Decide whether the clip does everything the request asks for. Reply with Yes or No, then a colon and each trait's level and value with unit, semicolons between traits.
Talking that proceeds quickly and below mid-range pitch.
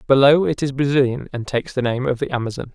Yes: fast, 240 wpm; low, 130 Hz